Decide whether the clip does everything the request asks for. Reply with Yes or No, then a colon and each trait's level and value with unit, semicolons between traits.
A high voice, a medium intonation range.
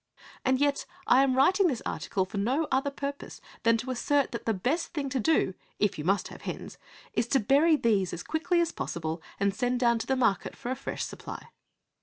Yes: very high, 255 Hz; average, 4.8 semitones